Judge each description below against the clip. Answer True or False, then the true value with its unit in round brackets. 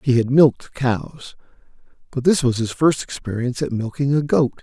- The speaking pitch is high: False (130 Hz)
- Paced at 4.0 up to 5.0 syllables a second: False (5.5 syllables/s)